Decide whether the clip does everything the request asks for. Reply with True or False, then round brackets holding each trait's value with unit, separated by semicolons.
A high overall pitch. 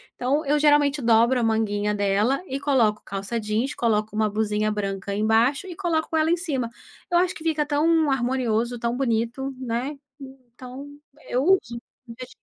True (245 Hz)